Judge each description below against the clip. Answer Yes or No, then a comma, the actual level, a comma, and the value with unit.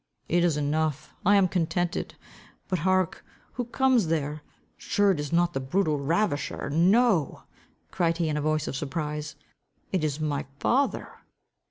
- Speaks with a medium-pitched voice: Yes, medium, 165 Hz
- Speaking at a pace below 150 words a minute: No, average, 155 wpm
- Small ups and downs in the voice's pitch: No, average, 3.9 semitones